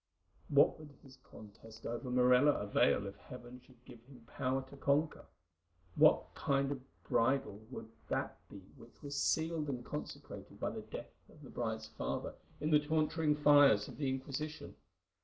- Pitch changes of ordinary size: Yes, average, 3.7 semitones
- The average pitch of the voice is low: Yes, low, 130 Hz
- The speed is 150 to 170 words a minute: Yes, average, 165 wpm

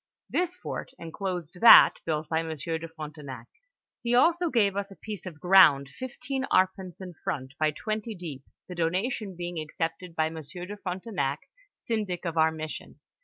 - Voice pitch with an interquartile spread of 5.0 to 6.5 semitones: No, average, 4.4 semitones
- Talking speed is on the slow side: No, average, 165 wpm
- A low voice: No, medium, 175 Hz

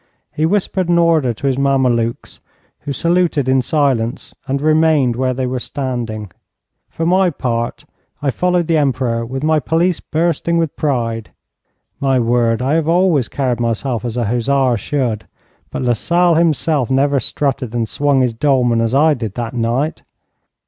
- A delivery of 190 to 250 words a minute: No, average, 160 wpm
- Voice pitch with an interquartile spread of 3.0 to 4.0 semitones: No, average, 4.6 semitones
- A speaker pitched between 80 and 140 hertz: Yes, low, 135 Hz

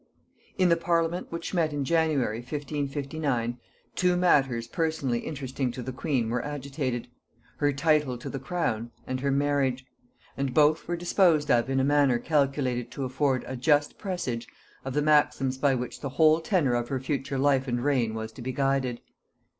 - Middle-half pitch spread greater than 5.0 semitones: No, average, 3.2 semitones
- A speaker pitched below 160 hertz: Yes, medium, 140 Hz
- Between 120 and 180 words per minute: Yes, average, 175 wpm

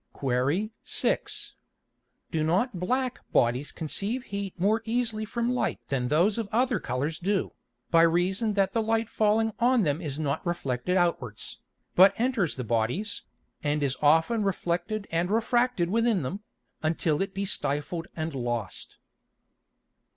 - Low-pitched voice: No, medium, 185 Hz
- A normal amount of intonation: No, wide, 6.5 semitones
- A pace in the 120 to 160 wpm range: Yes, average, 145 wpm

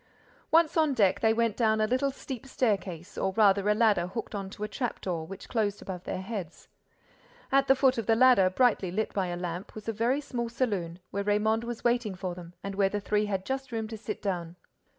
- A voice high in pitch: Yes, high, 210 Hz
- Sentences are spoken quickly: Yes, fast, 230 wpm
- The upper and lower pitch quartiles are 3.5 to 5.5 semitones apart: Yes, average, 3.8 semitones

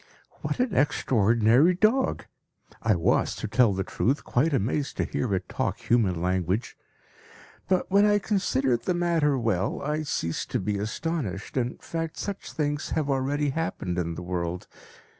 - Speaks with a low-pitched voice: Yes, low, 130 Hz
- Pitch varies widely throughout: Yes, wide, 8.5 semitones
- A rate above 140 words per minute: Yes, average, 160 wpm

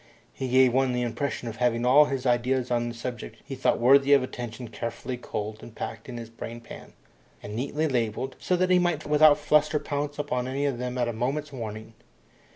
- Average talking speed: No, fast, 210 wpm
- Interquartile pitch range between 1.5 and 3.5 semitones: Yes, average, 3.2 semitones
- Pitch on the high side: No, low, 125 Hz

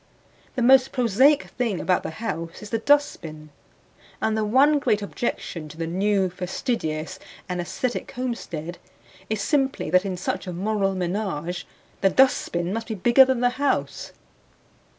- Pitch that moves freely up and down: Yes, wide, 5.9 semitones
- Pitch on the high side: Yes, high, 205 Hz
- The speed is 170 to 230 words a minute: No, average, 150 wpm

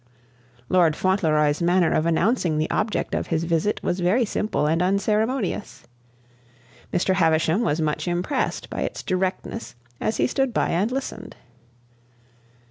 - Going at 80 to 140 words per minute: Yes, slow, 135 wpm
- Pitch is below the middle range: No, medium, 180 Hz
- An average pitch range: Yes, average, 4.7 semitones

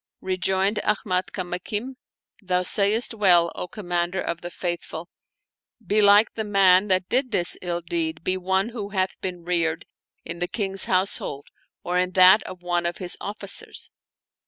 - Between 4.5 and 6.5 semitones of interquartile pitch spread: No, narrow, 2.4 semitones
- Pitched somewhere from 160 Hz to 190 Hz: Yes, medium, 185 Hz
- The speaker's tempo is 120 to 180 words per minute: Yes, average, 160 wpm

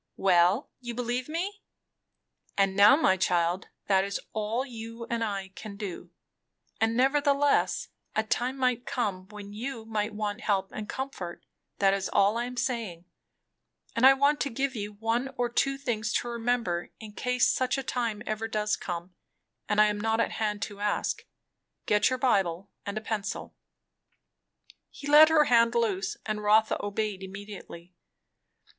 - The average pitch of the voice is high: Yes, high, 220 Hz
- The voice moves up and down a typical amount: Yes, average, 3.6 semitones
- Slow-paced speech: No, average, 165 wpm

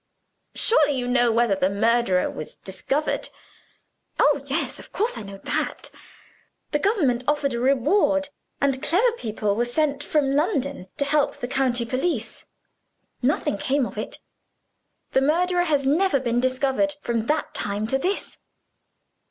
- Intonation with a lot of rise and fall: No, average, 4.0 semitones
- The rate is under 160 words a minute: Yes, average, 145 wpm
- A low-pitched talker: No, very high, 270 Hz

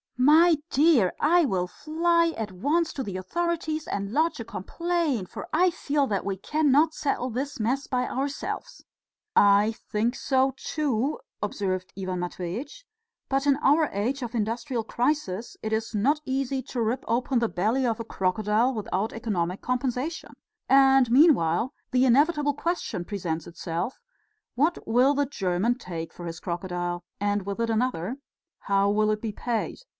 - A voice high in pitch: Yes, high, 240 Hz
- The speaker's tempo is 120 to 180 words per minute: Yes, average, 155 wpm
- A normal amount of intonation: No, wide, 6.1 semitones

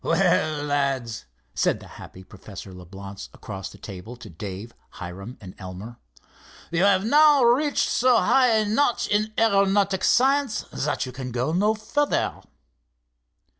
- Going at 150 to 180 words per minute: No, average, 140 wpm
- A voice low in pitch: No, medium, 145 Hz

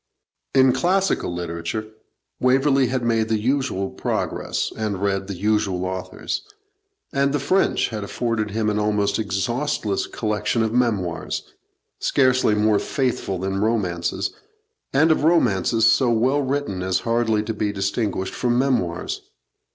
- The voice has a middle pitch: No, low, 110 Hz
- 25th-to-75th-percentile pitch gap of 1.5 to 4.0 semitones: No, average, 4.7 semitones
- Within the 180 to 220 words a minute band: No, slow, 135 wpm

